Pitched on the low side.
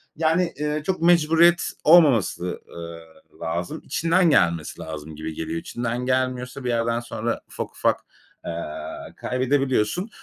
Yes: low, 125 Hz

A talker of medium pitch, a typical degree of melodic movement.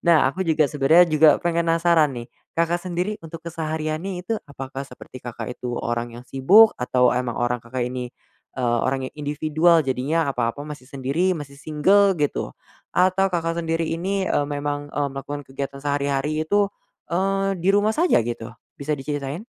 Yes: medium, 150 Hz; average, 4.2 semitones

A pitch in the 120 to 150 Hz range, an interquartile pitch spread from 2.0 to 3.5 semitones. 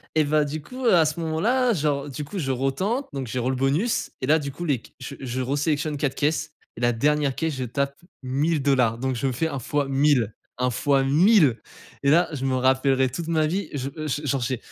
Yes: medium, 140 Hz; average, 3.0 semitones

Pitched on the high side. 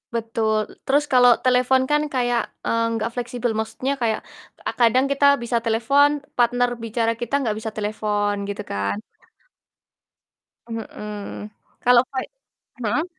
Yes: high, 235 Hz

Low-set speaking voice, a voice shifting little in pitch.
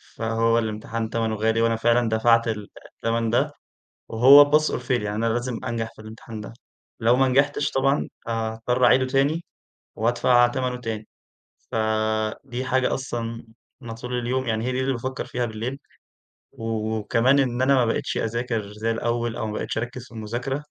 Yes: low, 120 Hz; narrow, 2.2 semitones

